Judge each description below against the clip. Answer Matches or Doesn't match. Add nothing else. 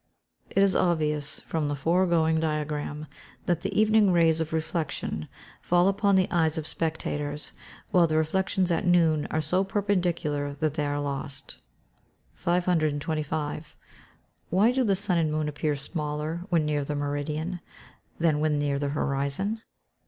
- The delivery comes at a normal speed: Matches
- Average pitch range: Matches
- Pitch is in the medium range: Matches